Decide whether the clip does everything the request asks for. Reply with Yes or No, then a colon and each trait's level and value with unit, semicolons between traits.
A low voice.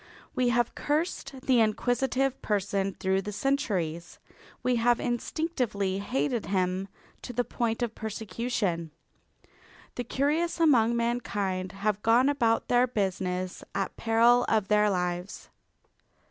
No: high, 225 Hz